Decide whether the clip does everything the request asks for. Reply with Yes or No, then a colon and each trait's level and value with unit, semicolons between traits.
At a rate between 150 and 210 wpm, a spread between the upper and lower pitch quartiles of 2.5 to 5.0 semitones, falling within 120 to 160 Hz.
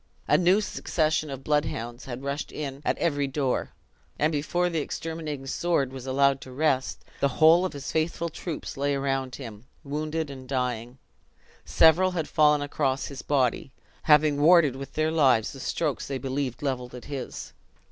Yes: average, 170 wpm; average, 2.9 semitones; medium, 140 Hz